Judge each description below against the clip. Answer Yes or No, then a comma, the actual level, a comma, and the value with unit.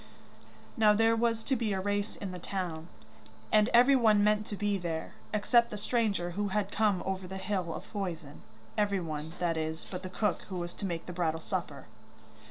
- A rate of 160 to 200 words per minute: Yes, average, 190 wpm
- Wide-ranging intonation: No, average, 3.4 semitones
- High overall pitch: Yes, high, 195 Hz